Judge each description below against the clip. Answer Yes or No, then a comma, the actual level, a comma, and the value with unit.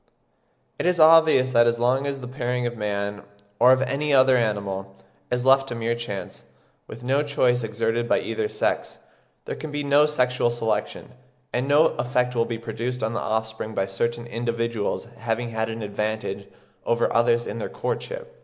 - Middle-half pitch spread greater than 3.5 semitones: No, narrow, 2.6 semitones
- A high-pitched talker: No, low, 120 Hz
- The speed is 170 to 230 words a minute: Yes, average, 180 wpm